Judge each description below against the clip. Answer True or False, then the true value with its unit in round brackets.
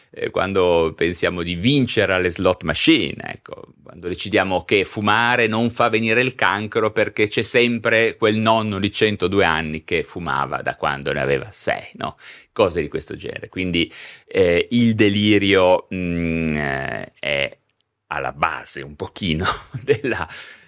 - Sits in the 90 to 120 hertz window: True (100 Hz)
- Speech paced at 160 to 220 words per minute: False (140 wpm)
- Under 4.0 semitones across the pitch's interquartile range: False (4.4 semitones)